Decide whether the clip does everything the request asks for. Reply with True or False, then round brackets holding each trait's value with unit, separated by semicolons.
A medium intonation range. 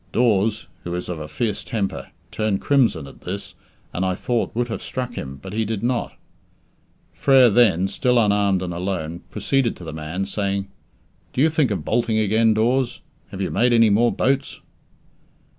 True (4.3 semitones)